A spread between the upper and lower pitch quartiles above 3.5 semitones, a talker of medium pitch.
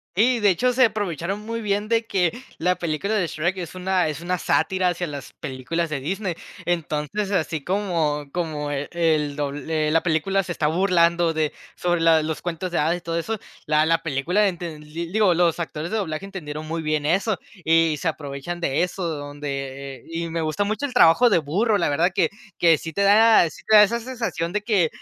Yes: average, 4.1 semitones; medium, 170 Hz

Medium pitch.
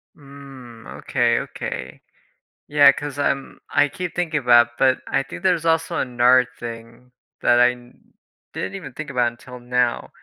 No: low, 130 Hz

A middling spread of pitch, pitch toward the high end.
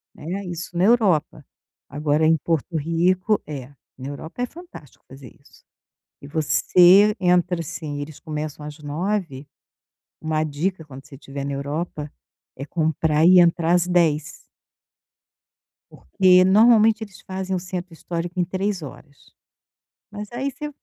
No: average, 3.9 semitones; medium, 170 Hz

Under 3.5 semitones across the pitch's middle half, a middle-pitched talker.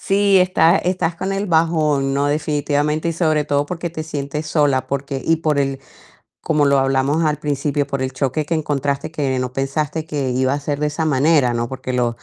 Yes: narrow, 2.6 semitones; medium, 145 Hz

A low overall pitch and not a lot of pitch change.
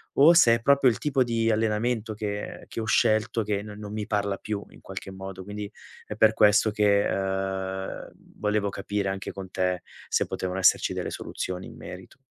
Yes: low, 105 Hz; narrow, 2.2 semitones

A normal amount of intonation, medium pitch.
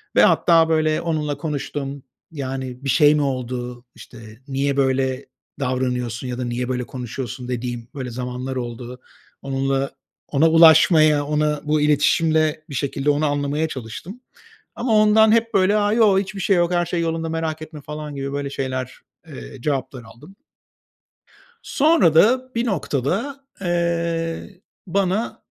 Yes: average, 4.4 semitones; medium, 145 Hz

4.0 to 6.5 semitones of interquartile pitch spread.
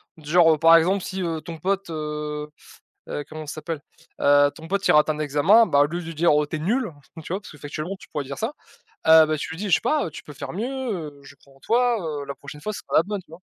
Yes: average, 4.3 semitones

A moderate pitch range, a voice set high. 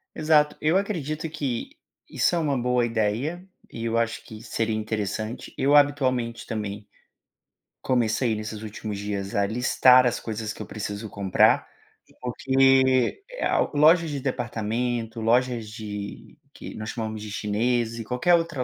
No: average, 3.5 semitones; low, 115 Hz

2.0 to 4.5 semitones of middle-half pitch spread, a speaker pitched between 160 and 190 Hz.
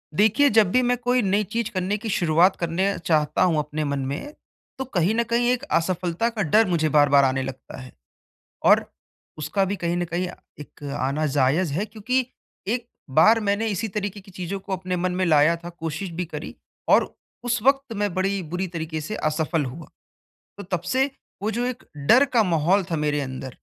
No: wide, 5.4 semitones; medium, 185 Hz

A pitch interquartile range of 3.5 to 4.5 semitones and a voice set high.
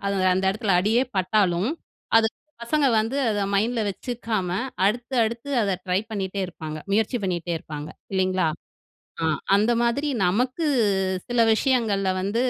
Yes: average, 4.0 semitones; high, 210 Hz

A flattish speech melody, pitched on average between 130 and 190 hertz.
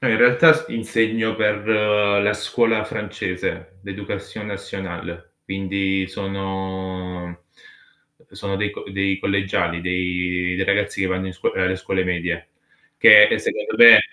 No: narrow, 2.3 semitones; very low, 95 Hz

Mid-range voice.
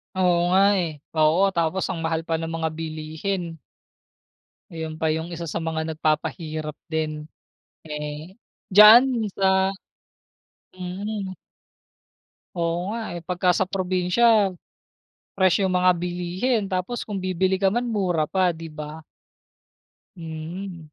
Yes: medium, 175 Hz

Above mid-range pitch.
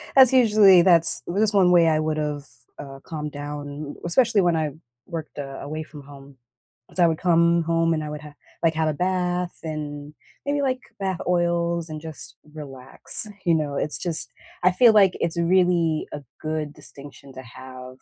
No: medium, 160 Hz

